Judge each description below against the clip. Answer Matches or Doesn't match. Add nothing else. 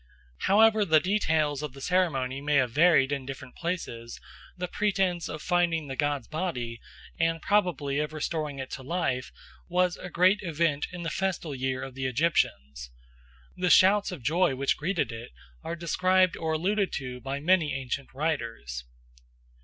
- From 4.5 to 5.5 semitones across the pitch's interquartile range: Matches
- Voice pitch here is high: Doesn't match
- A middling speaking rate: Matches